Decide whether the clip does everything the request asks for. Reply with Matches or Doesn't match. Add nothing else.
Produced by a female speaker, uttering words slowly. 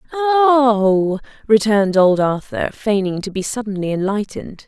Matches